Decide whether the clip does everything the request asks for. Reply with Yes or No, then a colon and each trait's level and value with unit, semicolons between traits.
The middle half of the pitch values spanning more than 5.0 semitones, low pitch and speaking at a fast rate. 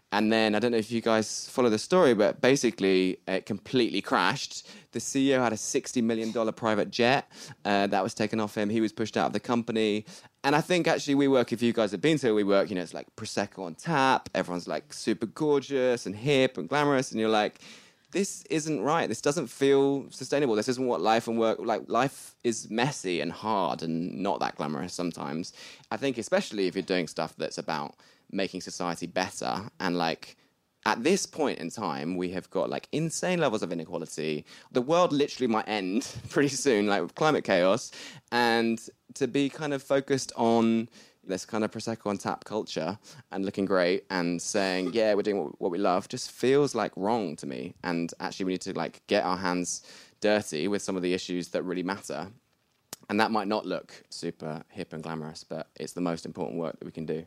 Yes: wide, 5.6 semitones; low, 110 Hz; fast, 210 wpm